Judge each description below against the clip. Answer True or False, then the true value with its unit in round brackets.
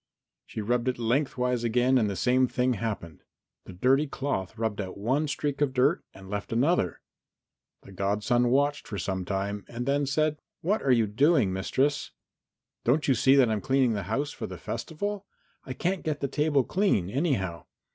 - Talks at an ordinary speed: True (180 wpm)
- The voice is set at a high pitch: False (125 Hz)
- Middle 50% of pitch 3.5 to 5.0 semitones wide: False (5.5 semitones)